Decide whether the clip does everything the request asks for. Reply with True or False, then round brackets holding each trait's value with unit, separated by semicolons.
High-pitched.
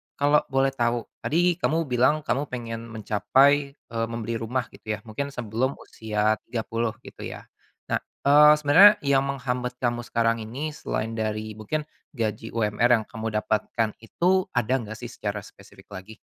False (120 Hz)